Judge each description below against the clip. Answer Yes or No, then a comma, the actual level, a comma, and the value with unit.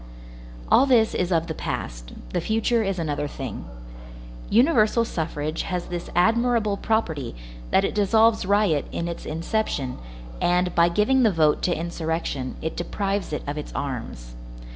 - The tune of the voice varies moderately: No, wide, 5.9 semitones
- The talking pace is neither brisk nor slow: Yes, average, 150 wpm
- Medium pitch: Yes, medium, 175 Hz